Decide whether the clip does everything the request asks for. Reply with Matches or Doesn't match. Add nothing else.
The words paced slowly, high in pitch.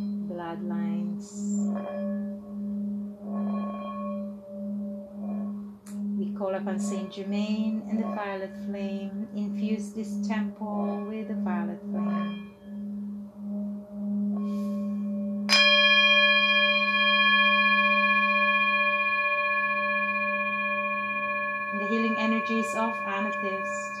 Matches